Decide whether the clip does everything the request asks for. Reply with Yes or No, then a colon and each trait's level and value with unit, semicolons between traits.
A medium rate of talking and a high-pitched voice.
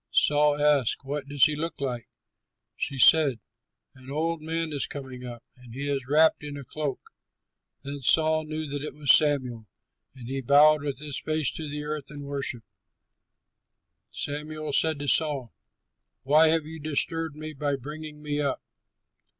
No: average, 165 wpm; medium, 145 Hz